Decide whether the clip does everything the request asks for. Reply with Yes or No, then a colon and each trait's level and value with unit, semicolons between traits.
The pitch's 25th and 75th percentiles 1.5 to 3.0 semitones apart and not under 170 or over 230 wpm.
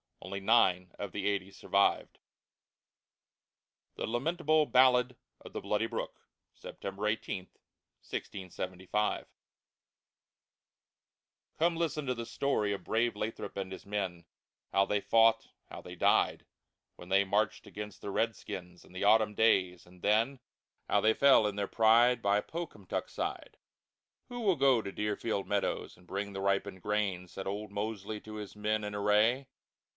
No: narrow, 2.6 semitones; average, 150 wpm